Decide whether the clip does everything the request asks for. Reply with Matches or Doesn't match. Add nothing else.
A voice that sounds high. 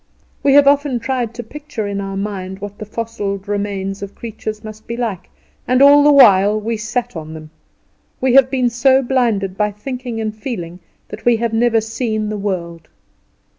Matches